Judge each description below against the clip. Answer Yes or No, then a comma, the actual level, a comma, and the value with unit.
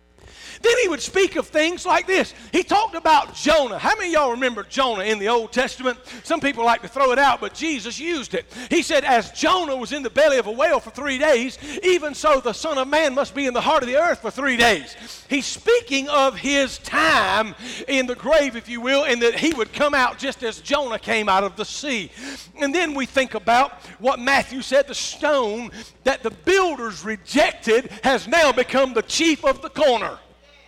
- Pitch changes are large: No, average, 4.5 semitones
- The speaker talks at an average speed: No, fast, 215 wpm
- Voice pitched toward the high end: Yes, very high, 270 Hz